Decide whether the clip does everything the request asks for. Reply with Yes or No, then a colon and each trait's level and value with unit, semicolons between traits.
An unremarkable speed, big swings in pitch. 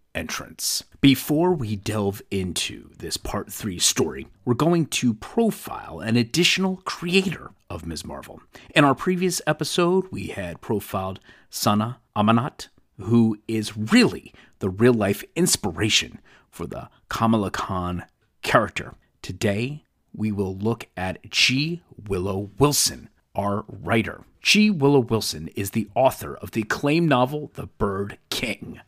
No: slow, 130 wpm; wide, 6.3 semitones